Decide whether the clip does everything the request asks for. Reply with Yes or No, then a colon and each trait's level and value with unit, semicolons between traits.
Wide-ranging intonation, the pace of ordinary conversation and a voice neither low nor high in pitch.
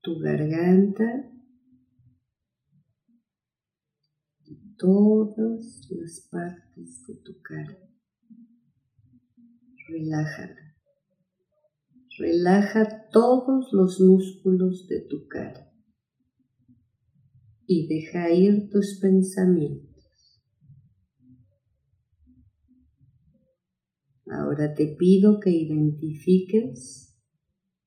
No: wide, 8.1 semitones; slow, 60 wpm; medium, 165 Hz